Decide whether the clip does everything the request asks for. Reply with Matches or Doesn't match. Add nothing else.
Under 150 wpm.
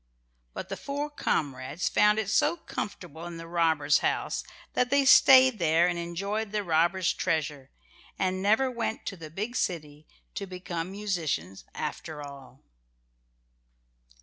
Matches